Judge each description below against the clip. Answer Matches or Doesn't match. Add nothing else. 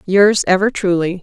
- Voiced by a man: Doesn't match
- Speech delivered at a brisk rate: Doesn't match